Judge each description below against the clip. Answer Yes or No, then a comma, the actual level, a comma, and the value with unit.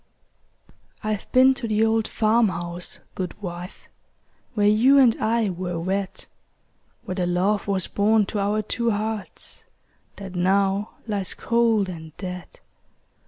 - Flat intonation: No, average, 3.1 semitones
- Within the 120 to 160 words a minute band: Yes, slow, 135 wpm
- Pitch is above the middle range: Yes, high, 205 Hz